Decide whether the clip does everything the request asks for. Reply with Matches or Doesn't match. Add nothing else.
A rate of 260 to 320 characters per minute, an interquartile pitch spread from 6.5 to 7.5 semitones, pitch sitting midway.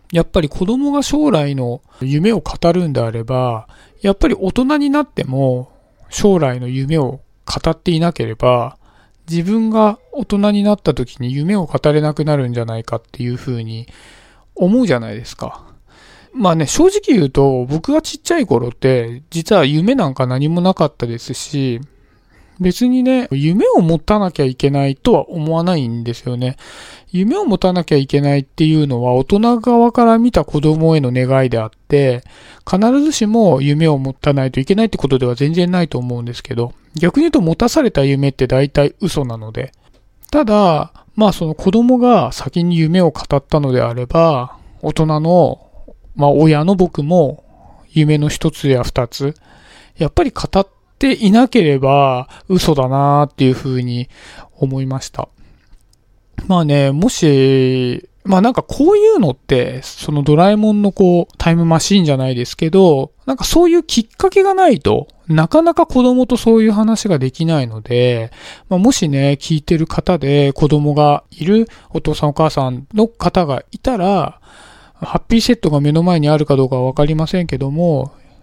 Matches